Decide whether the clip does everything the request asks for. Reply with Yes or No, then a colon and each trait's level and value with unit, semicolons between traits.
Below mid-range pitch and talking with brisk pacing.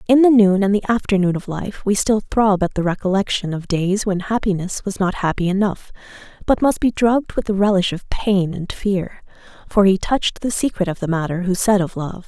No: high, 195 Hz; fast, 220 wpm